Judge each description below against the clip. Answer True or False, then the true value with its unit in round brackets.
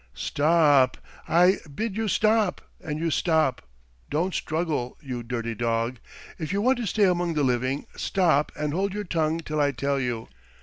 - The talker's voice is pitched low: False (155 Hz)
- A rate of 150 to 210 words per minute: True (175 wpm)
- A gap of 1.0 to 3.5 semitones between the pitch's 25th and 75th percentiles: False (5.4 semitones)